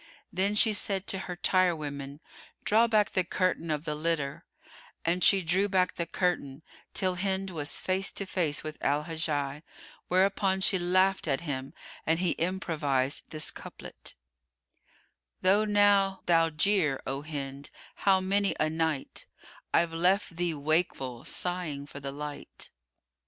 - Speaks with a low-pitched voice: No, medium, 170 Hz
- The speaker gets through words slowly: No, average, 145 wpm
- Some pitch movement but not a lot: Yes, average, 4.2 semitones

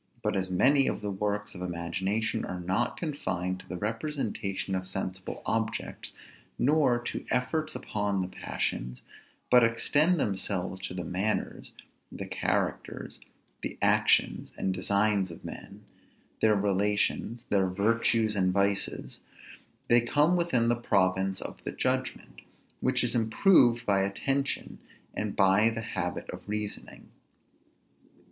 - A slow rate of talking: Yes, slow, 130 wpm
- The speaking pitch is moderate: No, low, 105 Hz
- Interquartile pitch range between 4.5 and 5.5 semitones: No, average, 3.9 semitones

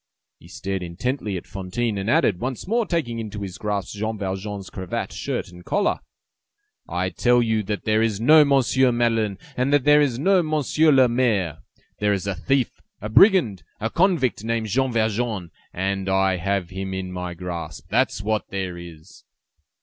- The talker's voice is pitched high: No, low, 110 Hz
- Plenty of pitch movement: No, average, 4.9 semitones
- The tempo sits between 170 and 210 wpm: Yes, average, 175 wpm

